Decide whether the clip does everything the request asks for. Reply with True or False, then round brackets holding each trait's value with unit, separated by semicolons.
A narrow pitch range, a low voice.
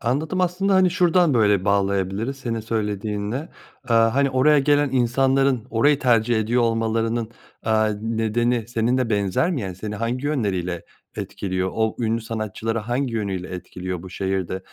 False (4.1 semitones; 115 Hz)